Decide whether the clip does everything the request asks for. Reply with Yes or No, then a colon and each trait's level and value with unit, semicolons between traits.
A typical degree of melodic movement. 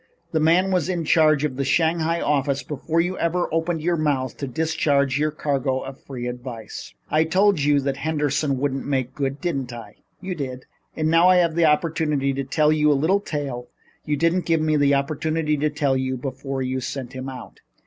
Yes: average, 3.2 semitones